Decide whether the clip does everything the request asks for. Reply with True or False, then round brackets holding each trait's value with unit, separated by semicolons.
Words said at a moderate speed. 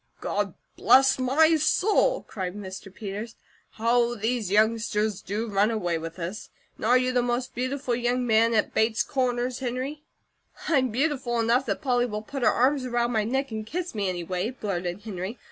True (175 wpm)